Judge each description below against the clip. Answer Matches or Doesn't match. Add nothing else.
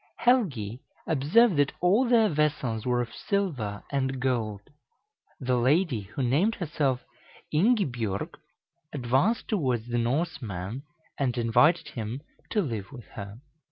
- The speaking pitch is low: Matches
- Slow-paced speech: Matches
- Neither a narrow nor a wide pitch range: Doesn't match